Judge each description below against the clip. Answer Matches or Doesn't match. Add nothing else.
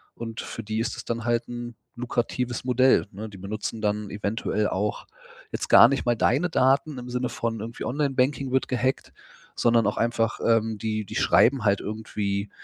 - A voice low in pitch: Matches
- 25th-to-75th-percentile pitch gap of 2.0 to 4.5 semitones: Matches